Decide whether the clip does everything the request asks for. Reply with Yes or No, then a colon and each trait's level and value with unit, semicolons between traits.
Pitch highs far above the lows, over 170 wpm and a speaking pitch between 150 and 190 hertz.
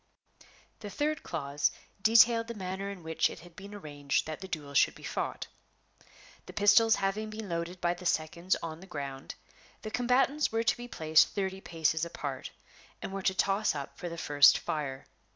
No: average, 5.0 semitones; average, 185 wpm; medium, 185 Hz